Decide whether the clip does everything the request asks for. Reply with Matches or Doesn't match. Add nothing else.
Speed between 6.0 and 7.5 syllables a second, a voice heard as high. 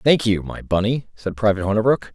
Doesn't match